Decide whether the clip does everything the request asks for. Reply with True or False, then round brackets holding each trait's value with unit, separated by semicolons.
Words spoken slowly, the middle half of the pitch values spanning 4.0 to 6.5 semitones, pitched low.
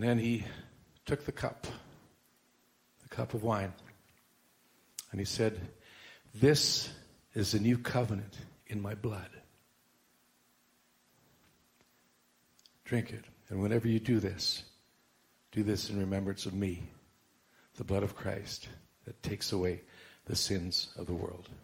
False (130 wpm; 3.0 semitones; 105 Hz)